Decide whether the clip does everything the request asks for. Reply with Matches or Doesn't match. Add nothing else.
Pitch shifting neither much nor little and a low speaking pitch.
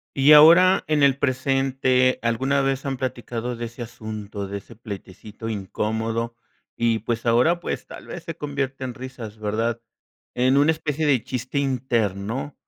Matches